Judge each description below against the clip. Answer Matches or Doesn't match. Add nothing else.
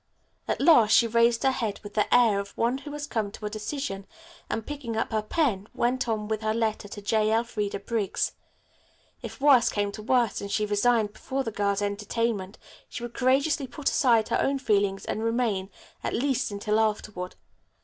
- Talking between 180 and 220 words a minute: Matches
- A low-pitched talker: Doesn't match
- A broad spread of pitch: Doesn't match